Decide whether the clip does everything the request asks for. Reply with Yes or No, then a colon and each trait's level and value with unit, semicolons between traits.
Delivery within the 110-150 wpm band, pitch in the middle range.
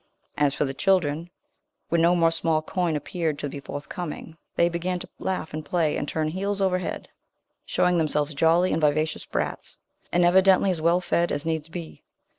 No: average, 185 wpm; medium, 165 Hz